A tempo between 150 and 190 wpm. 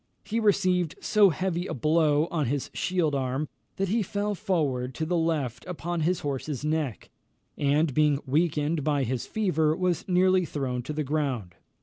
Yes: average, 165 wpm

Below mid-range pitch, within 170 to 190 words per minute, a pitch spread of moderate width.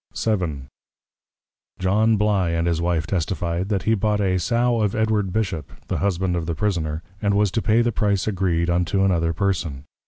Yes: very low, 95 Hz; average, 180 wpm; average, 3.7 semitones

